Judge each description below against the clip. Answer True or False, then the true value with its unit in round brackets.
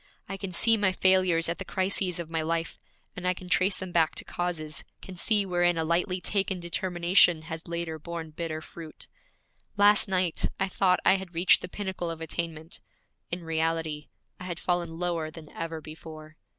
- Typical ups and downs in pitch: False (2.2 semitones)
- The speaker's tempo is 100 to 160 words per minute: False (185 wpm)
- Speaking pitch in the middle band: True (175 Hz)